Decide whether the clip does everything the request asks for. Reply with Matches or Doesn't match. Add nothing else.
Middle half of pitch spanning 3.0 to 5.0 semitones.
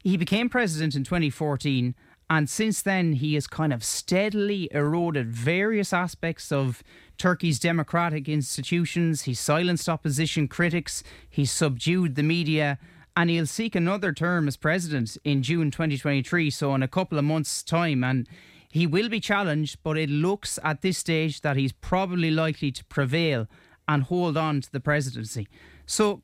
Matches